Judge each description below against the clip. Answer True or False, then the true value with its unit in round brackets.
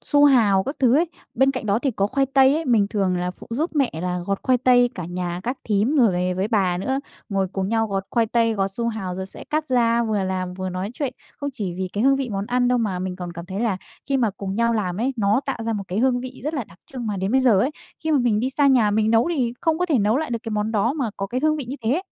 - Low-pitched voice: False (225 Hz)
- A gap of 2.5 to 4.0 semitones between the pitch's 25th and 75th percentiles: False (5.0 semitones)